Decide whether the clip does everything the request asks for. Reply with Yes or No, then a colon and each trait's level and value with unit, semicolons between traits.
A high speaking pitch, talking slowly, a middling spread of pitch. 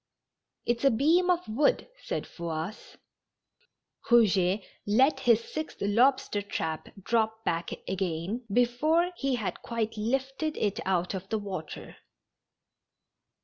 No: high, 225 Hz; slow, 115 wpm; wide, 5.7 semitones